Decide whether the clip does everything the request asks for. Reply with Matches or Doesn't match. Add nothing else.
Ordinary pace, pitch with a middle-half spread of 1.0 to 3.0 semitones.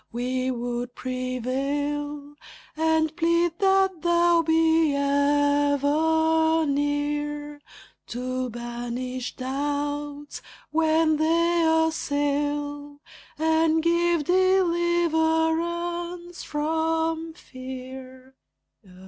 Doesn't match